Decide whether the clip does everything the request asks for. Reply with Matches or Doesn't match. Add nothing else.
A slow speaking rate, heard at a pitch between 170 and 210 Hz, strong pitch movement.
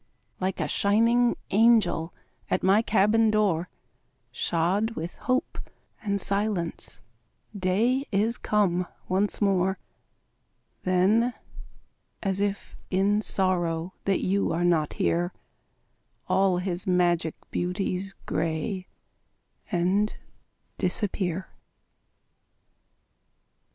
Doesn't match